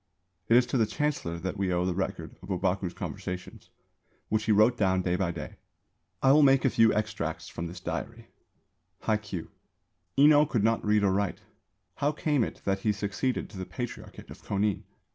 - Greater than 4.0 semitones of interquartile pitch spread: Yes, average, 4.6 semitones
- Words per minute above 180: Yes, average, 190 wpm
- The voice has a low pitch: Yes, low, 105 Hz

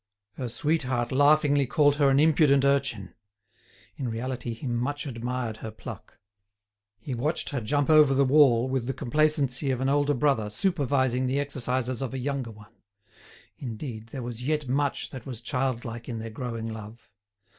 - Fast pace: No, average, 165 wpm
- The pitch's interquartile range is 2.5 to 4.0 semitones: Yes, average, 3.3 semitones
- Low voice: Yes, low, 130 Hz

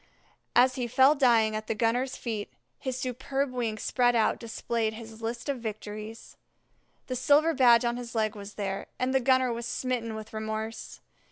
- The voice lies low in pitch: No, high, 235 Hz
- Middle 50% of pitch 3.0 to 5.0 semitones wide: No, narrow, 2.6 semitones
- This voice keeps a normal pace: Yes, average, 175 wpm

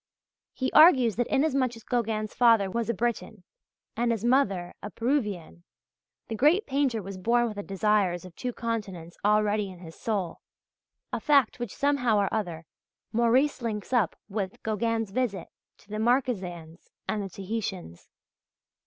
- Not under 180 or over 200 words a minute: No, average, 155 wpm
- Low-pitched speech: No, high, 220 Hz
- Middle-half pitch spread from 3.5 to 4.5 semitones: Yes, average, 3.8 semitones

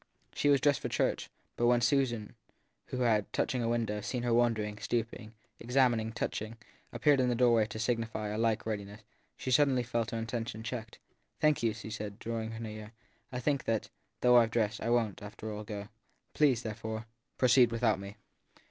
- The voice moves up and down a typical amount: No, narrow, 2.1 semitones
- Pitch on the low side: Yes, low, 115 Hz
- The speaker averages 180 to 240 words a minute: Yes, average, 190 wpm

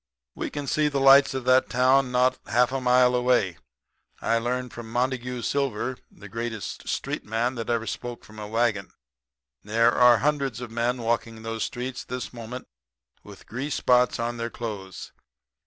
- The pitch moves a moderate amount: No, narrow, 1.9 semitones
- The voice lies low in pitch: Yes, low, 120 Hz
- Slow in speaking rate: No, average, 170 wpm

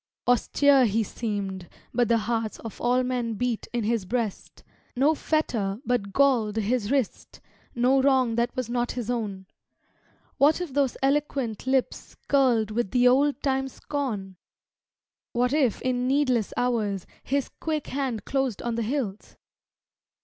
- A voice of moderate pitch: No, high, 245 Hz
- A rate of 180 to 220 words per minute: No, average, 145 wpm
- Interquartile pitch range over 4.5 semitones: No, average, 3.4 semitones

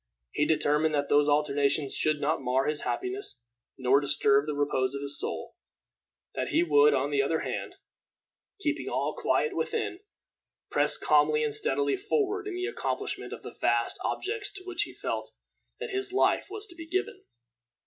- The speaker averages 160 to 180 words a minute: Yes, average, 170 wpm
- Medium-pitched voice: Yes, medium, 155 Hz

